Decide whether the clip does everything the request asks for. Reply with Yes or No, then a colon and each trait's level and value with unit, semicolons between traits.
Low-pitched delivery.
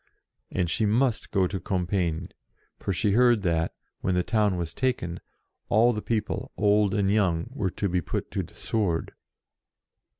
Yes: low, 100 Hz